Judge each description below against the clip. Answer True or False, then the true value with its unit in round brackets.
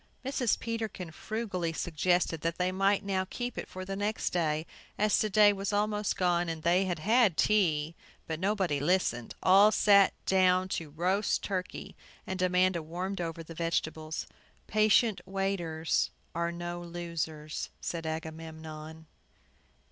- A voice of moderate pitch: True (180 Hz)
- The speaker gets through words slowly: False (145 wpm)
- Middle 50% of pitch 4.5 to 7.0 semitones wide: False (3.4 semitones)